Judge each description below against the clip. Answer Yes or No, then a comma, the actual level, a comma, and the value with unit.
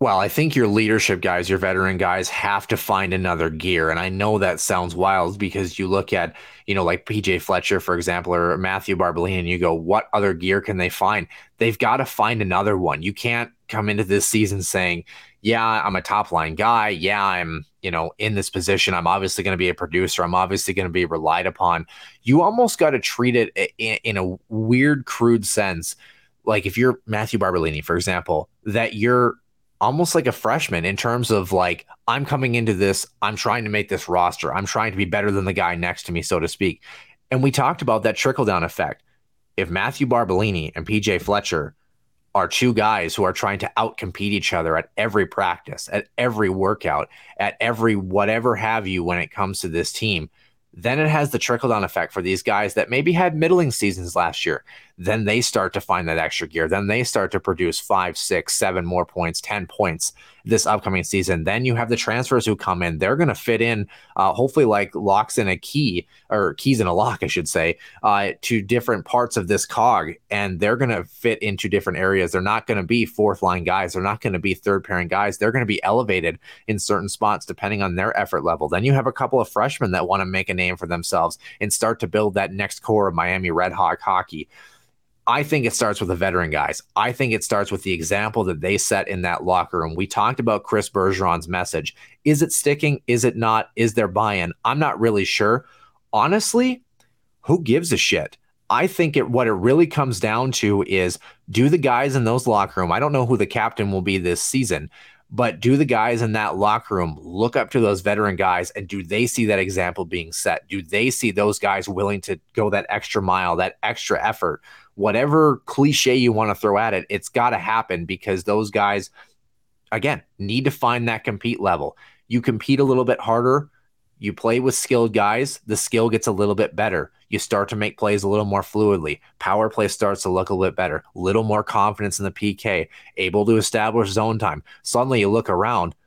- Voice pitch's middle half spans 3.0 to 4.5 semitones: Yes, average, 4.0 semitones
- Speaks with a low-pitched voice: Yes, low, 105 Hz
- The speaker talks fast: Yes, fast, 220 wpm